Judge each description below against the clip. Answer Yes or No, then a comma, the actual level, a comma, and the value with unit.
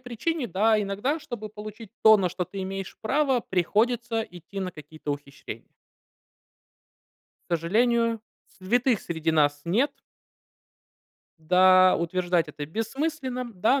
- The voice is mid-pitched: No, high, 205 Hz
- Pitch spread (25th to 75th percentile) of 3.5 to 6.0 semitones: Yes, average, 5.3 semitones